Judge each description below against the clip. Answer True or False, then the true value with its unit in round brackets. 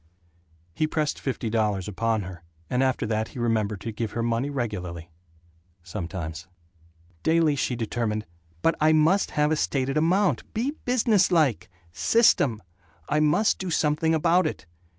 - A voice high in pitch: False (130 Hz)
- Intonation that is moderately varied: False (6.7 semitones)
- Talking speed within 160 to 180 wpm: False (150 wpm)